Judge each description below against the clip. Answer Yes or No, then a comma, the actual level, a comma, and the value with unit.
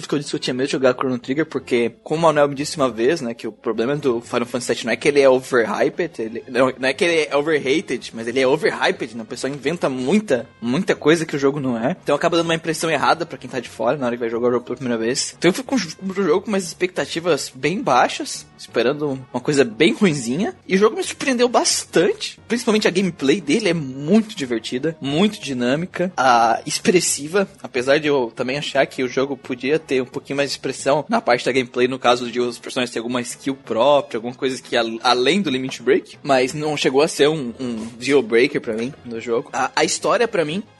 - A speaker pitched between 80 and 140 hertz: Yes, low, 135 Hz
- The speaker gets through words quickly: Yes, fast, 240 wpm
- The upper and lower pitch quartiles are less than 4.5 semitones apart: No, average, 4.8 semitones